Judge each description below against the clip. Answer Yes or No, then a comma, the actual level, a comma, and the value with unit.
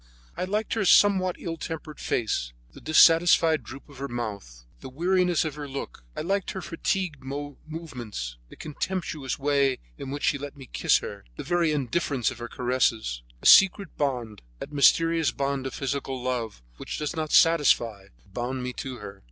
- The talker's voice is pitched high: No, medium, 140 Hz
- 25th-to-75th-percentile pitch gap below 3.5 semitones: No, average, 4.8 semitones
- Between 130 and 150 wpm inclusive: No, average, 175 wpm